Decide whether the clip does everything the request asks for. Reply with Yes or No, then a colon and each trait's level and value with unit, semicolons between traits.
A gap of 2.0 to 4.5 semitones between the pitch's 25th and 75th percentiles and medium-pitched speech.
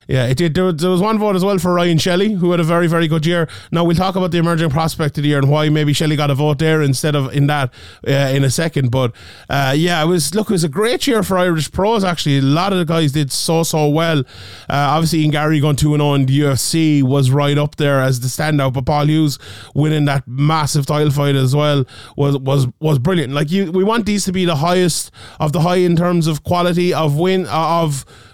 Yes: average, 3.6 semitones; medium, 155 Hz